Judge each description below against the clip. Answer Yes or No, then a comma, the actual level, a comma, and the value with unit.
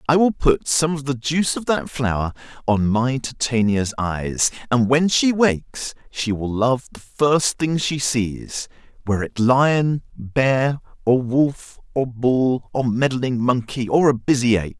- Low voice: Yes, low, 130 Hz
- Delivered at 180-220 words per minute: No, average, 165 wpm